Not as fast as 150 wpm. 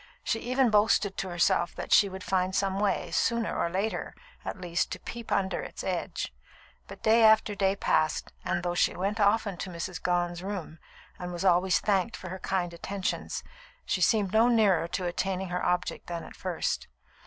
No: average, 190 wpm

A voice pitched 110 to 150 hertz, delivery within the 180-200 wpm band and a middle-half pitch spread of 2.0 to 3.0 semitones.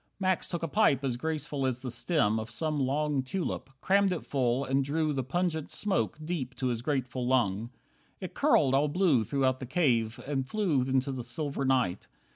No: low, 135 Hz; average, 190 wpm; average, 3.7 semitones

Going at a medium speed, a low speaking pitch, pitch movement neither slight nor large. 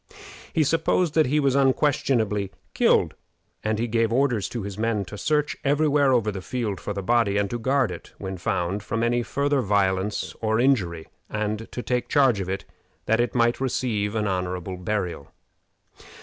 Yes: average, 180 wpm; low, 110 Hz; average, 4.8 semitones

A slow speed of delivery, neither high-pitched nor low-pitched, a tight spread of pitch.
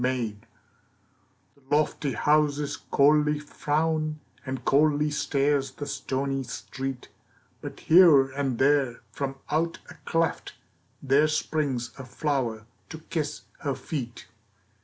Yes: slow, 110 wpm; medium, 145 Hz; narrow, 2.2 semitones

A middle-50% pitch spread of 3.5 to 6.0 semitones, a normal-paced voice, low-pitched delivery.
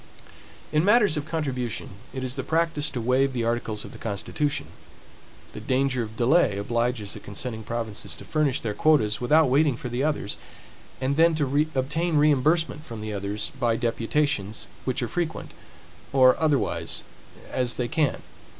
Yes: average, 4.6 semitones; average, 160 wpm; low, 130 Hz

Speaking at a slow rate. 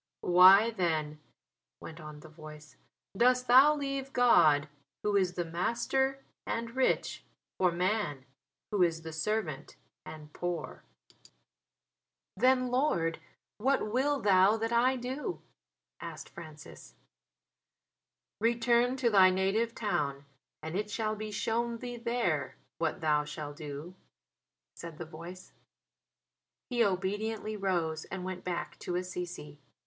Yes: slow, 125 wpm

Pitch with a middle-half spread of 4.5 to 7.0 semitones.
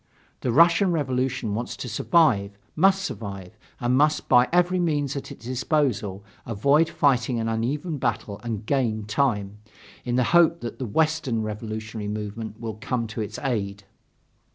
Yes: average, 5.2 semitones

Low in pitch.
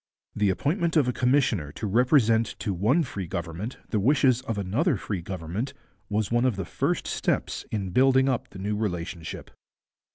Yes: low, 110 Hz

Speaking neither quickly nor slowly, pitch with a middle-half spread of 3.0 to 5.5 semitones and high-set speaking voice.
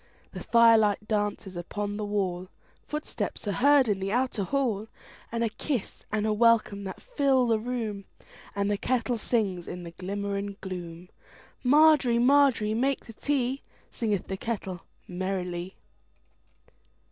No: slow, 125 wpm; average, 4.0 semitones; high, 215 Hz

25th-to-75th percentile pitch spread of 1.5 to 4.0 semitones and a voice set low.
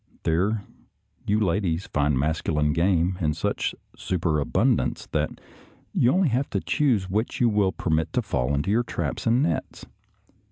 No: wide, 5.4 semitones; very low, 90 Hz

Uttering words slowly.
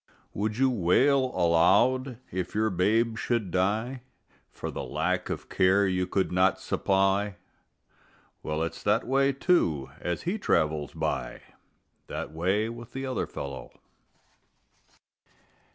Yes: slow, 125 wpm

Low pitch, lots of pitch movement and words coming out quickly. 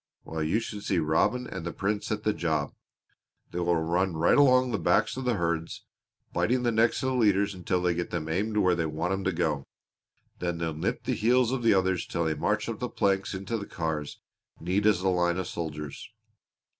No: very low, 90 Hz; average, 4.3 semitones; fast, 220 wpm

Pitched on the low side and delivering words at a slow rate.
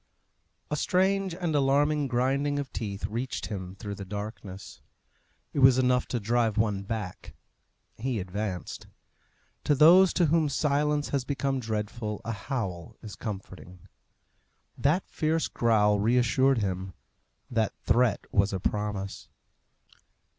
Yes: low, 120 Hz; slow, 125 wpm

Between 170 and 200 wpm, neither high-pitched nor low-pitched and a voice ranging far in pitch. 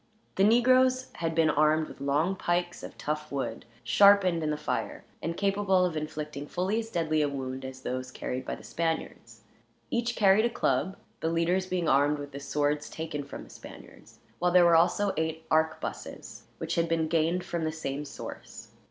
No: average, 185 wpm; medium, 160 Hz; average, 3.6 semitones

